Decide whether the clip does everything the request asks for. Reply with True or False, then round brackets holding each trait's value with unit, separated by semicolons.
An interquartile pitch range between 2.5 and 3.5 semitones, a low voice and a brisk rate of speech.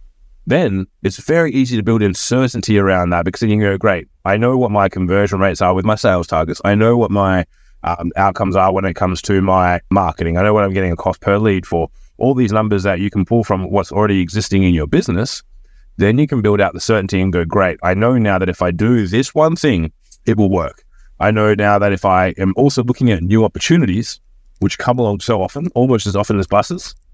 True (2.9 semitones; 100 Hz; 240 wpm)